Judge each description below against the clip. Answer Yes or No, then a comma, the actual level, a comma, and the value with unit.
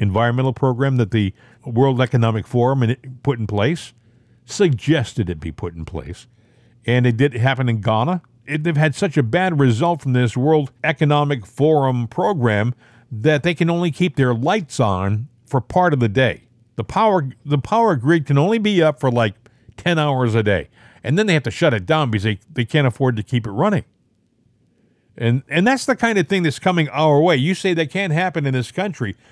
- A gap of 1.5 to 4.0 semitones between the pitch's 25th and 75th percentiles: No, average, 5.1 semitones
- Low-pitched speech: Yes, low, 130 Hz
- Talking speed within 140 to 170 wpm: No, fast, 205 wpm